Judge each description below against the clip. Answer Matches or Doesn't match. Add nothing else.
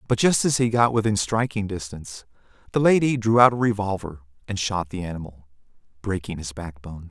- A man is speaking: Matches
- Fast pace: Doesn't match